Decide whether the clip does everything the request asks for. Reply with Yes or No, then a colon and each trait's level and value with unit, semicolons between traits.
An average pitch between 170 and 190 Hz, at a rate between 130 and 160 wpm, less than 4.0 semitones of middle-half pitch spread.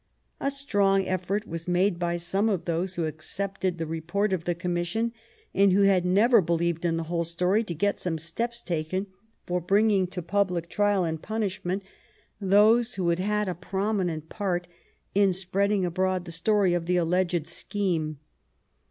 No: medium, 185 Hz; average, 170 wpm; average, 2.8 semitones